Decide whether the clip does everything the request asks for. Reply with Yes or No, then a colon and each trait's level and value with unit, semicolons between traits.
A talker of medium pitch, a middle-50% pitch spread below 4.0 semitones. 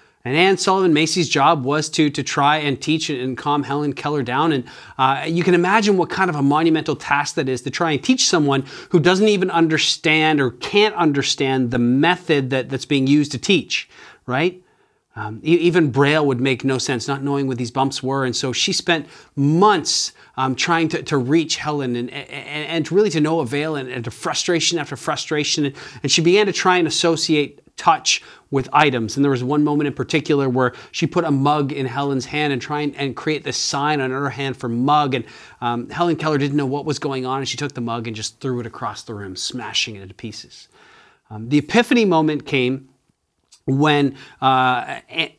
Yes: medium, 145 Hz; average, 3.3 semitones